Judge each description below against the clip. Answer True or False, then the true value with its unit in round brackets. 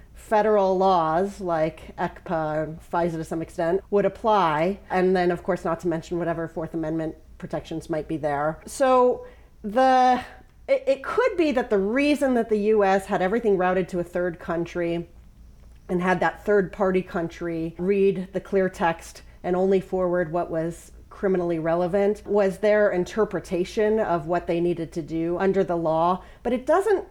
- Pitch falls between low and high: True (180 Hz)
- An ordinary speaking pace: True (165 wpm)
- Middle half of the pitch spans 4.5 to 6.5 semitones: False (3.4 semitones)